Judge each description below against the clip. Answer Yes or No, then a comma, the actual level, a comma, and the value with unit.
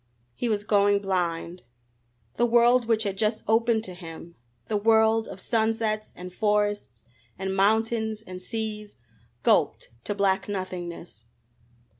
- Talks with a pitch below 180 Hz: No, high, 205 Hz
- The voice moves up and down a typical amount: Yes, average, 3.0 semitones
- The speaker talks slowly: Yes, slow, 130 wpm